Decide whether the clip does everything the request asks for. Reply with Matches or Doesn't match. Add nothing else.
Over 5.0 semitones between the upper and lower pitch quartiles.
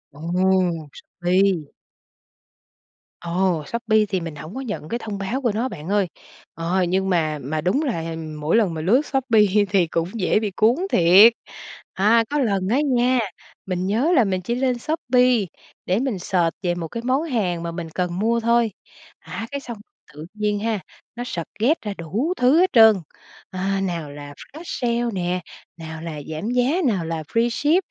Matches